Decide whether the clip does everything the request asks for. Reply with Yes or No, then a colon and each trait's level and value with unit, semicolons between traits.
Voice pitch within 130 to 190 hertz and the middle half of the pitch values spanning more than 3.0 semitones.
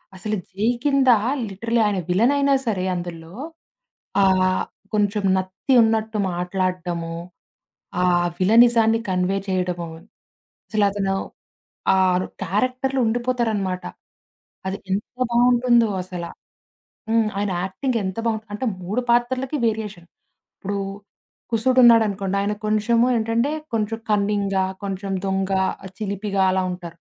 No: high, 205 Hz; average, 3.6 semitones